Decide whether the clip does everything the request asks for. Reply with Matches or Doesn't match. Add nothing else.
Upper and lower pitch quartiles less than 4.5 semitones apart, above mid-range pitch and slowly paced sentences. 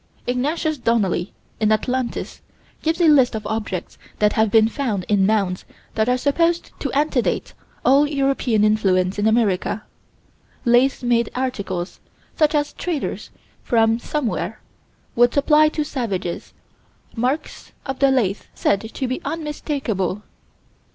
Doesn't match